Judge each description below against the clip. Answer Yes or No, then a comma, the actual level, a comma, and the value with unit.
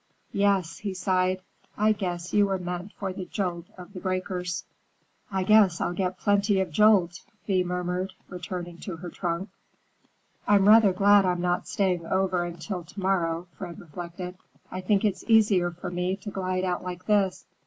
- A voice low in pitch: No, medium, 185 Hz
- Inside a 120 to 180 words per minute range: Yes, average, 170 wpm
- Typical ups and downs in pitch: No, narrow, 1.9 semitones